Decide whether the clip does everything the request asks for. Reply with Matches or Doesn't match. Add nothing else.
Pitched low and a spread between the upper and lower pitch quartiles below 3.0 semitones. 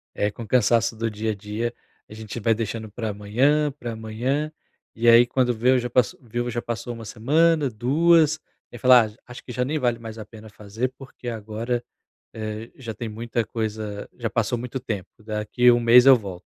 Matches